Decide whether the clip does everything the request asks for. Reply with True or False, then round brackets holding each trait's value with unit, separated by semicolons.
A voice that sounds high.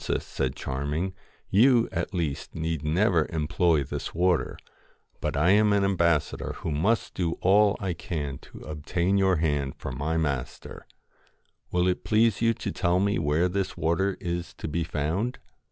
False (85 Hz)